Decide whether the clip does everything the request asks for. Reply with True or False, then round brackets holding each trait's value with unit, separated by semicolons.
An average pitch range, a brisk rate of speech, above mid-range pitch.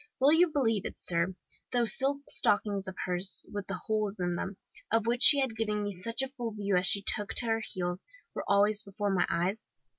True (3.2 semitones; 215 wpm; 210 Hz)